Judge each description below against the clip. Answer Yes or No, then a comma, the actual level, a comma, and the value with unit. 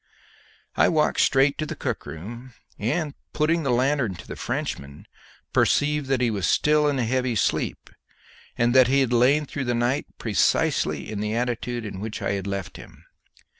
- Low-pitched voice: Yes, low, 120 Hz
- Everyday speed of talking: Yes, average, 180 wpm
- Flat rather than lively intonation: No, average, 4.7 semitones